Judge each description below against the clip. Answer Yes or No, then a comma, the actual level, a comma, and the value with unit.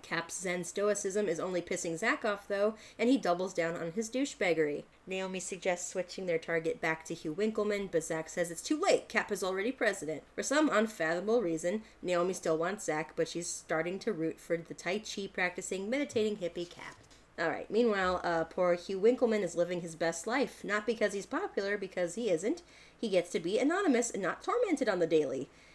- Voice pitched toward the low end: No, medium, 185 Hz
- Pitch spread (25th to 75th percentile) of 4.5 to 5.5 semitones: No, average, 4.1 semitones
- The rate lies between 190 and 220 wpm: Yes, average, 200 wpm